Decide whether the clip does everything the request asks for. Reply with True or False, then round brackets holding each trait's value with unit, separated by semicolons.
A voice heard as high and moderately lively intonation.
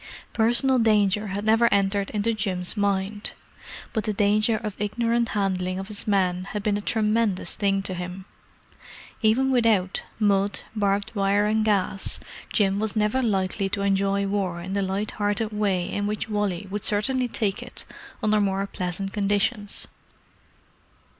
False (205 Hz; 1.7 semitones)